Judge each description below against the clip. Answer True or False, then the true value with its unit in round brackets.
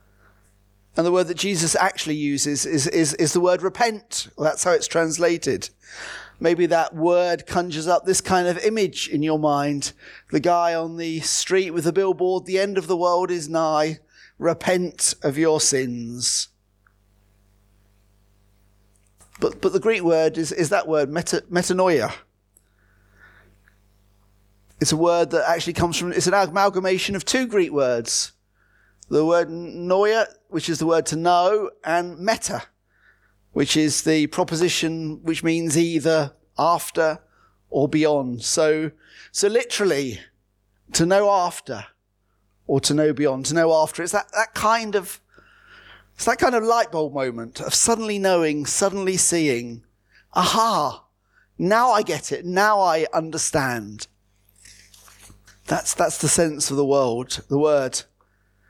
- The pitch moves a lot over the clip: True (6.9 semitones)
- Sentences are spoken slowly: False (145 wpm)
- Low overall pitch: False (160 Hz)